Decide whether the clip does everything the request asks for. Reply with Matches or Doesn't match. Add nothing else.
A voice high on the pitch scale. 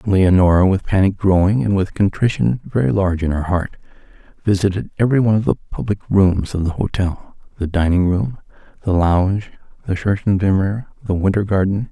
Doesn't match